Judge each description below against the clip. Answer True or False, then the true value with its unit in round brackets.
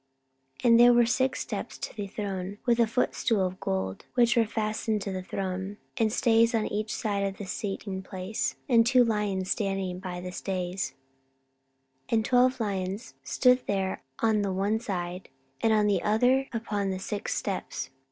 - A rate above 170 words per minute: True (180 wpm)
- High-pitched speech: True (205 Hz)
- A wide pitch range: False (3.2 semitones)